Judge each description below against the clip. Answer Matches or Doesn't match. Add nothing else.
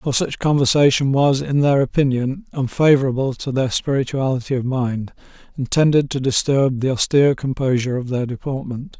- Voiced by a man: Matches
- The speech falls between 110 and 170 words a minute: Matches